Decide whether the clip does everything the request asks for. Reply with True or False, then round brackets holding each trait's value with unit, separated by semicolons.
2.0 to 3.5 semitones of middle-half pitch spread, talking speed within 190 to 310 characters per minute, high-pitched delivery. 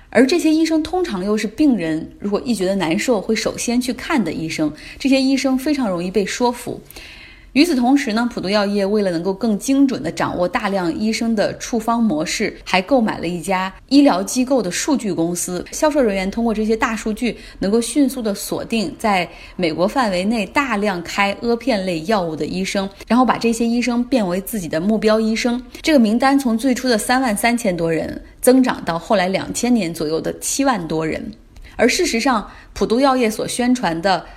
False (5.1 semitones; 300 characters per minute; 225 Hz)